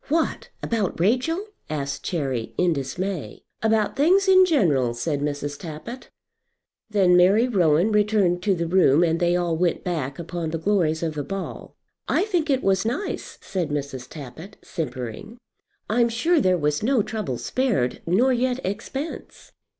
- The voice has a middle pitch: Yes, medium, 180 Hz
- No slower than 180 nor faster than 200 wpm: No, average, 155 wpm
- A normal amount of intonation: No, wide, 6.9 semitones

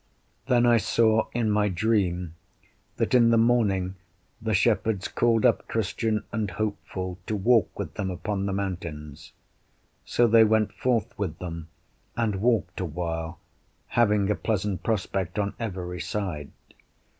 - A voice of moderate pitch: No, low, 105 Hz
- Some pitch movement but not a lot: Yes, average, 3.7 semitones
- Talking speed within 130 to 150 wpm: Yes, average, 145 wpm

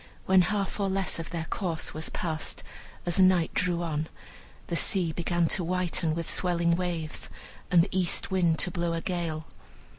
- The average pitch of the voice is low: No, medium, 175 Hz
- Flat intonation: Yes, narrow, 1.8 semitones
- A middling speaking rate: Yes, average, 175 wpm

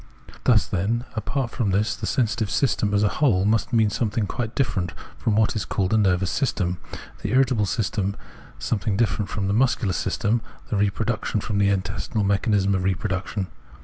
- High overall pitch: No, low, 105 Hz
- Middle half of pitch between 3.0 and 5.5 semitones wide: No, narrow, 2.6 semitones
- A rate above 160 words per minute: Yes, average, 180 wpm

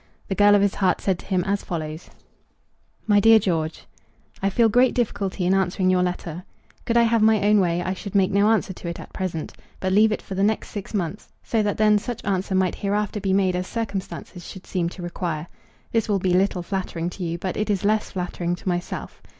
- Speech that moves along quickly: Yes, fast, 225 wpm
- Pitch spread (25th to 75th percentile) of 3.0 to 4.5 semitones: No, narrow, 2.6 semitones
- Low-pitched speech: No, high, 190 Hz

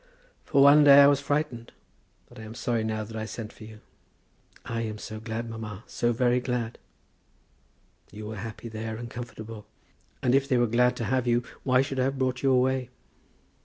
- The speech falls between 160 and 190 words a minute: No, average, 200 wpm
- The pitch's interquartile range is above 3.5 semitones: No, average, 2.7 semitones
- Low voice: Yes, low, 120 Hz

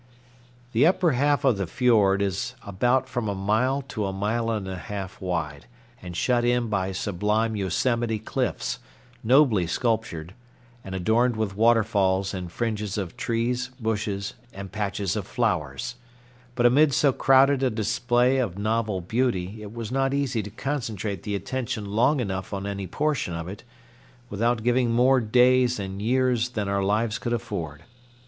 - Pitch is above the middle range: No, low, 110 Hz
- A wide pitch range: No, average, 3.9 semitones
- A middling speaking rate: Yes, average, 160 wpm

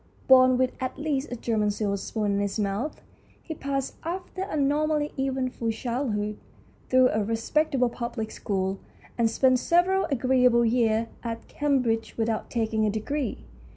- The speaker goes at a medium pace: Yes, average, 155 wpm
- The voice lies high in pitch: Yes, high, 245 Hz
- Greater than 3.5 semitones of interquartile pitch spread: Yes, average, 3.9 semitones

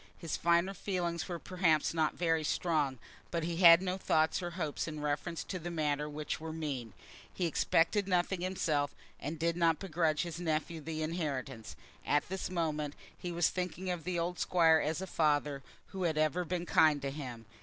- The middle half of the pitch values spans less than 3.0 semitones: Yes, narrow, 2.5 semitones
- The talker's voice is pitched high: No, medium, 165 Hz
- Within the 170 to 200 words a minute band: Yes, average, 185 wpm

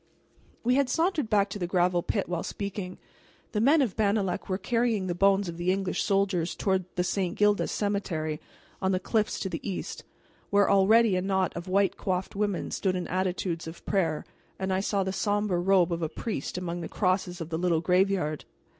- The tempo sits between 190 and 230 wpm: Yes, average, 200 wpm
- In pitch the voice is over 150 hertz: Yes, high, 190 Hz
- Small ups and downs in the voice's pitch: Yes, narrow, 2.3 semitones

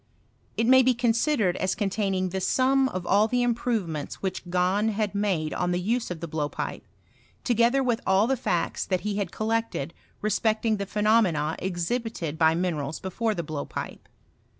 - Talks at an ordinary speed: Yes, average, 170 wpm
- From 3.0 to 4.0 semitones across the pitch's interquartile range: No, average, 4.5 semitones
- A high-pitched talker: Yes, high, 200 Hz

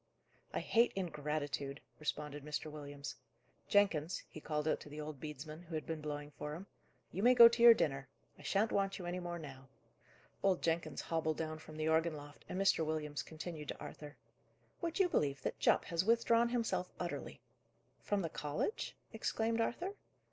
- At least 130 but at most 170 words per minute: No, average, 180 wpm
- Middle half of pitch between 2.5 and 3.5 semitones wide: No, average, 4.7 semitones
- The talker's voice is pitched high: No, medium, 160 Hz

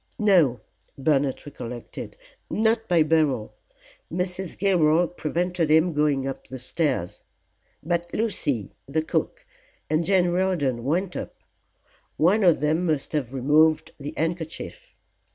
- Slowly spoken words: Yes, slow, 120 wpm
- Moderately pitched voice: Yes, medium, 160 Hz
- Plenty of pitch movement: No, average, 4.0 semitones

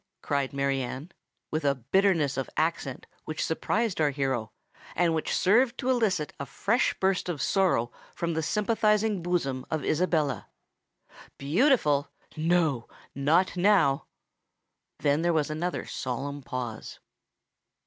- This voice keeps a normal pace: No, slow, 125 wpm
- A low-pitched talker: No, medium, 155 Hz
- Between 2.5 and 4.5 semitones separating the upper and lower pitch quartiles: No, average, 5.3 semitones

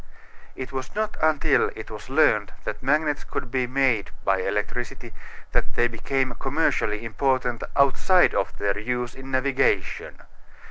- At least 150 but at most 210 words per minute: No, average, 140 wpm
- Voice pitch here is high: No, low, 130 Hz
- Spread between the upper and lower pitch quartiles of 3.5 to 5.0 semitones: No, average, 2.9 semitones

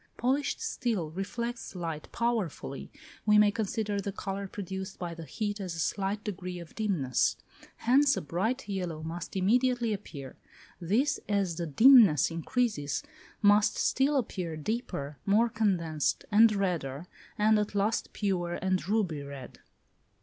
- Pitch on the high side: Yes, high, 195 Hz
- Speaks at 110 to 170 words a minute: Yes, average, 140 wpm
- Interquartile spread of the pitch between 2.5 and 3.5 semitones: No, average, 4.6 semitones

